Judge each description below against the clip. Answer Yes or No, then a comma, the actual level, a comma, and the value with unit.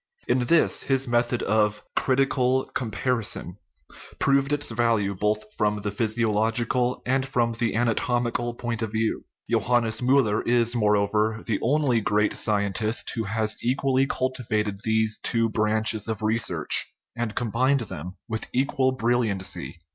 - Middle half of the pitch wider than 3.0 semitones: No, average, 2.7 semitones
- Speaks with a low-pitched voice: Yes, low, 115 Hz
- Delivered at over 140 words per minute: No, slow, 135 wpm